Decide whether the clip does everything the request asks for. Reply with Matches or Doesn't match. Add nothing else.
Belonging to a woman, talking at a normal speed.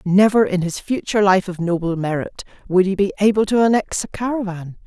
Matches